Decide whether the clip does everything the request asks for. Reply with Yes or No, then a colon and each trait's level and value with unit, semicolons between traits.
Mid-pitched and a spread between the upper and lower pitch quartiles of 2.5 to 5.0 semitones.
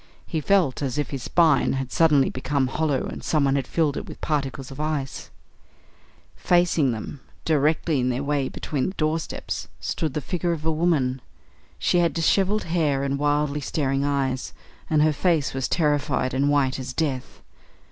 Yes: medium, 145 Hz; average, 3.0 semitones